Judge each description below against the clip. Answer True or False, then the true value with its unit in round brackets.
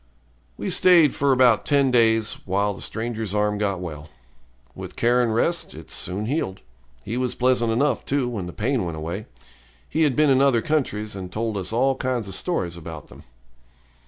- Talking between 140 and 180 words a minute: False (190 wpm)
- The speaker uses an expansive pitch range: False (4.8 semitones)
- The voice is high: False (115 Hz)